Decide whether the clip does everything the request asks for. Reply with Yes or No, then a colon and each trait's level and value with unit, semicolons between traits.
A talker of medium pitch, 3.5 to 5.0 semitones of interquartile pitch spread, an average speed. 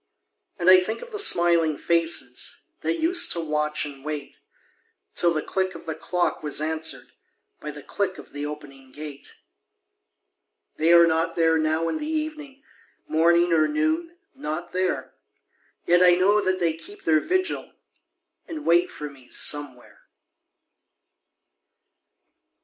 Yes: medium, 170 Hz; average, 4.0 semitones; average, 145 wpm